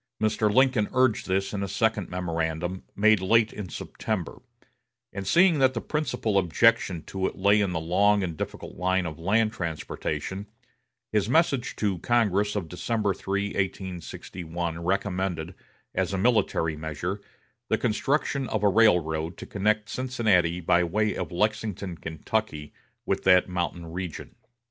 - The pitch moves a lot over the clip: No, average, 3.6 semitones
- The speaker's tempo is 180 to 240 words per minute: No, average, 145 wpm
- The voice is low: Yes, very low, 95 Hz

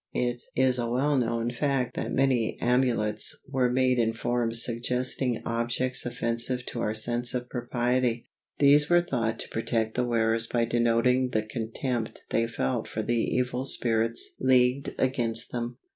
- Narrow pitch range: Yes, narrow, 1.6 semitones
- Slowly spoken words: No, average, 155 wpm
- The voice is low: Yes, low, 120 Hz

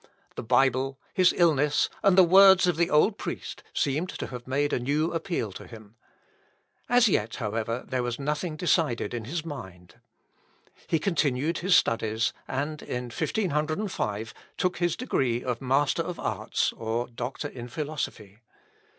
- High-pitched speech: No, medium, 140 Hz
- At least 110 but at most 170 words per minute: Yes, average, 150 wpm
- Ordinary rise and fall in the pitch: No, wide, 5.9 semitones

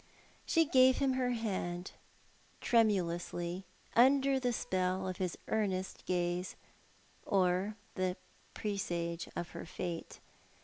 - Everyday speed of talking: No, slow, 105 wpm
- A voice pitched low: No, medium, 185 Hz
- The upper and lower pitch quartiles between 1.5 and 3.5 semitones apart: No, average, 4.8 semitones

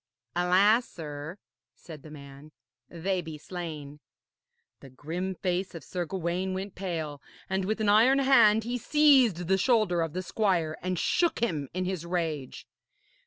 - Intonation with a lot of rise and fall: No, average, 4.3 semitones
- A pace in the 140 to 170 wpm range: Yes, average, 155 wpm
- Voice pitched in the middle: Yes, medium, 180 Hz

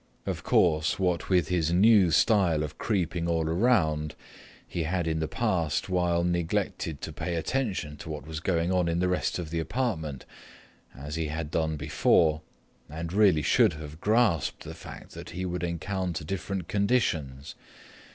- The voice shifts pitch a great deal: No, average, 2.9 semitones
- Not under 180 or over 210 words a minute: No, average, 165 wpm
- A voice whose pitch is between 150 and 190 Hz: No, very low, 85 Hz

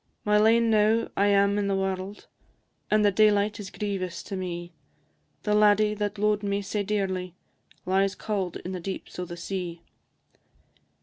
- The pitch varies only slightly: Yes, narrow, 2.0 semitones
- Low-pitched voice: No, high, 200 Hz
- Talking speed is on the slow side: No, average, 165 wpm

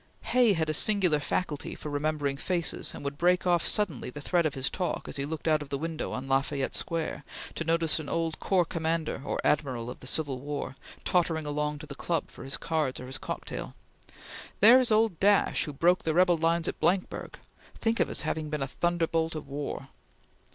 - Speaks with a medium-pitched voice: Yes, medium, 160 Hz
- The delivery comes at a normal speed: No, fast, 210 wpm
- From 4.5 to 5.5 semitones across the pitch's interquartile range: No, average, 3.2 semitones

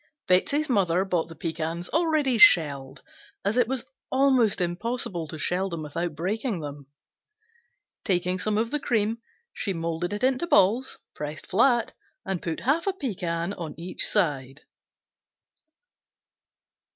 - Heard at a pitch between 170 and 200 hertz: Yes, high, 190 Hz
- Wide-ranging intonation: Yes, wide, 6.3 semitones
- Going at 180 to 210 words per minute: No, slow, 135 wpm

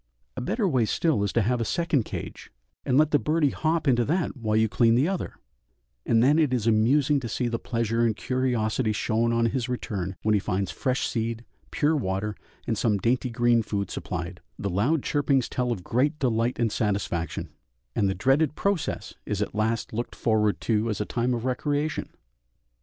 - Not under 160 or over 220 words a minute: Yes, average, 190 wpm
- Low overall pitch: Yes, low, 115 Hz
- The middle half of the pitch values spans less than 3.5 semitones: No, average, 3.9 semitones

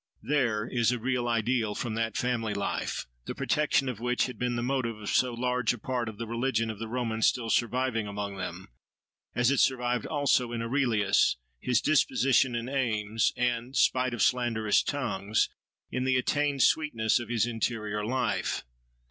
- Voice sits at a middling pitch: No, low, 120 Hz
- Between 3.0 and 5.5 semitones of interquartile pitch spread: No, narrow, 2.4 semitones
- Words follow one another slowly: No, average, 175 wpm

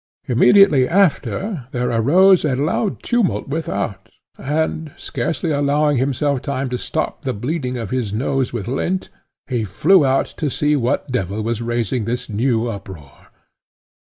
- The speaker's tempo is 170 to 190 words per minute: No, average, 145 wpm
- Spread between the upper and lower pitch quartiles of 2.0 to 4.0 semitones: No, average, 4.5 semitones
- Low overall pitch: Yes, low, 130 Hz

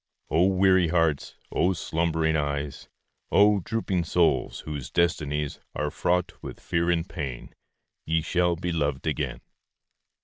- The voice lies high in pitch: No, very low, 85 Hz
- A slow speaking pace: Yes, slow, 130 wpm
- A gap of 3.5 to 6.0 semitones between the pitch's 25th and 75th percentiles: No, average, 3.0 semitones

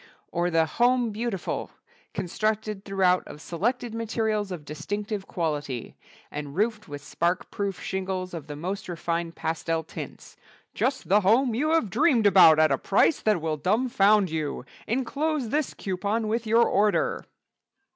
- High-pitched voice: Yes, high, 195 Hz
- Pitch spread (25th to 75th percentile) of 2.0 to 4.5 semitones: No, average, 5.2 semitones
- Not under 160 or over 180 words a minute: No, average, 145 wpm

